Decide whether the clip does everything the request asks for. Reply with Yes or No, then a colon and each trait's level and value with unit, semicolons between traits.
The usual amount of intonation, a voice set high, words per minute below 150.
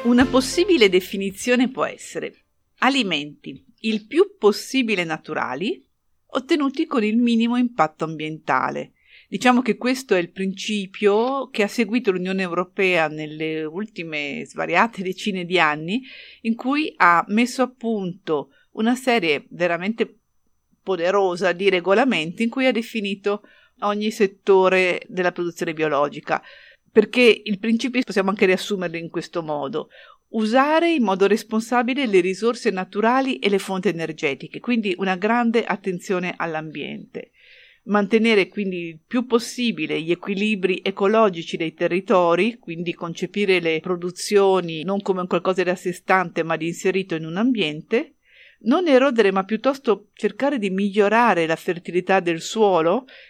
Yes: average, 4.8 semitones; high, 200 Hz; average, 130 wpm